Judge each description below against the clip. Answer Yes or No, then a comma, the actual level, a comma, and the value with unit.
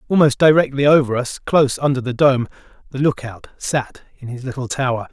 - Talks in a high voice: No, low, 130 Hz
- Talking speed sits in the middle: Yes, average, 175 wpm